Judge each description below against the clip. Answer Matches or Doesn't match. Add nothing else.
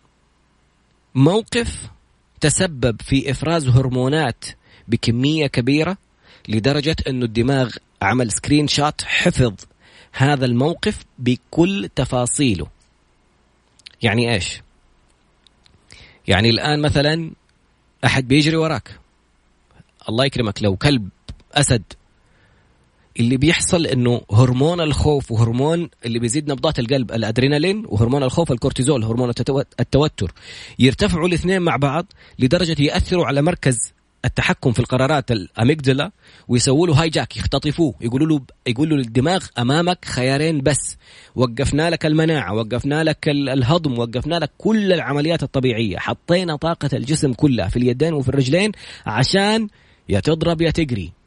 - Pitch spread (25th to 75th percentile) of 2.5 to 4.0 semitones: Doesn't match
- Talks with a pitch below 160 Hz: Matches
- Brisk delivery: Doesn't match